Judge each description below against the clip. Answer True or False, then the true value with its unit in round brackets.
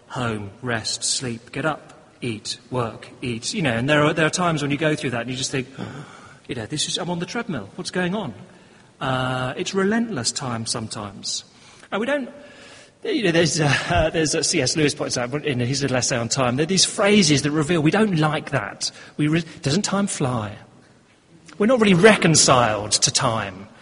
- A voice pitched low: False (145 Hz)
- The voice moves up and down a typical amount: False (6.0 semitones)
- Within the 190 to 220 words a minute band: True (205 wpm)